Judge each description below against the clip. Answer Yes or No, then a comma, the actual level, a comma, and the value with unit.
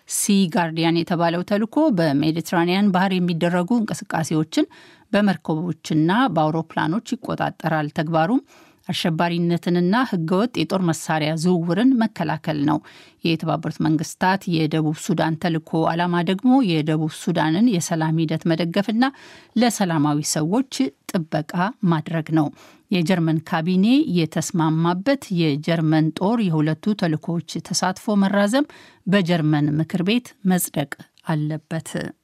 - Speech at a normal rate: Yes, average, 95 wpm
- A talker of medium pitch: Yes, medium, 175 Hz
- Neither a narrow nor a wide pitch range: Yes, average, 4.0 semitones